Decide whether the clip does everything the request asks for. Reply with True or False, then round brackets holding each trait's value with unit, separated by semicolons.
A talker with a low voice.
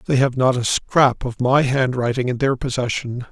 True (125 Hz)